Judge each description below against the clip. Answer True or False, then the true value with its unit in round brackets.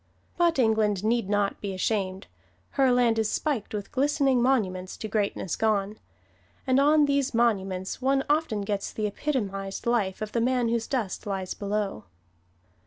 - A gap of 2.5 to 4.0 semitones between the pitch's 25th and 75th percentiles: False (4.5 semitones)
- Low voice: False (220 Hz)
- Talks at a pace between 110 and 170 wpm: True (155 wpm)